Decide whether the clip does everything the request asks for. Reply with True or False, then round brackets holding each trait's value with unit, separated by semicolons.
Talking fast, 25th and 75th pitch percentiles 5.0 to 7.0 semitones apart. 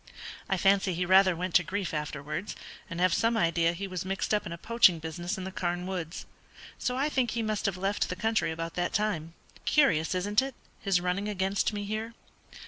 False (210 wpm; 3.3 semitones)